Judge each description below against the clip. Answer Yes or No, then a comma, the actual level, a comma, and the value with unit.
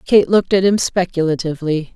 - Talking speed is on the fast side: No, average, 155 wpm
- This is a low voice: No, medium, 175 Hz